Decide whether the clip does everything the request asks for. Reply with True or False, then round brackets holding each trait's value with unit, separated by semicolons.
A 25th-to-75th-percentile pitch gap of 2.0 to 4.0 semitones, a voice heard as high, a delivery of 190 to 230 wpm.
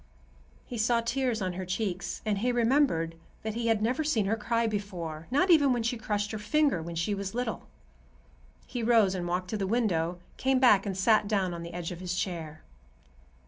False (4.5 semitones; 210 Hz; 205 wpm)